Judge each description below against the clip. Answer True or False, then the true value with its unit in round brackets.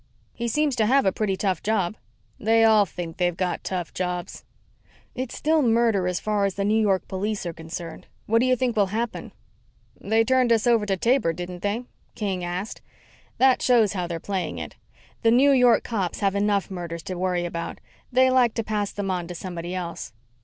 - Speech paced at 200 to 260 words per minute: True (205 wpm)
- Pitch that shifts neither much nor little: True (4.2 semitones)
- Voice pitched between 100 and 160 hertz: False (200 Hz)